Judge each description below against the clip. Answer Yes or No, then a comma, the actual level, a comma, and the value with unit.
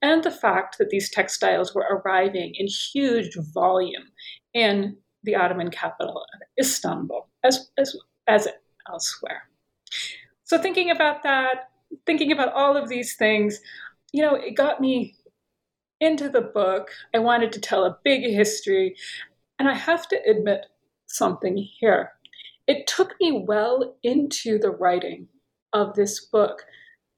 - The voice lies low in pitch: No, very high, 250 Hz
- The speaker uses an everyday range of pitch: No, wide, 6.4 semitones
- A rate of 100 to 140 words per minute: Yes, slow, 135 wpm